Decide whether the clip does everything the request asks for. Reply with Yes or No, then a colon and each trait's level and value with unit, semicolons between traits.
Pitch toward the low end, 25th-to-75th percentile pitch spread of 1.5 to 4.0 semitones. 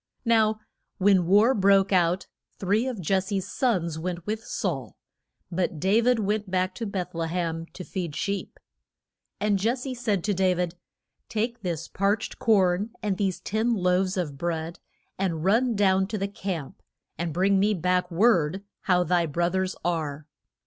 No: high, 190 Hz; average, 3.2 semitones